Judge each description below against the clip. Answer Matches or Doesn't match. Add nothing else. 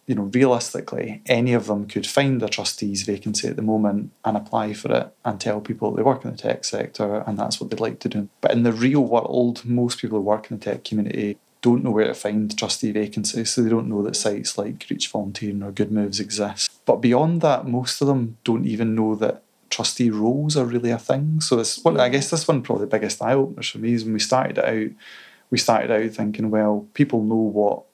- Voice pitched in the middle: Doesn't match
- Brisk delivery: Matches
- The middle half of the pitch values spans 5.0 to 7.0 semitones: Doesn't match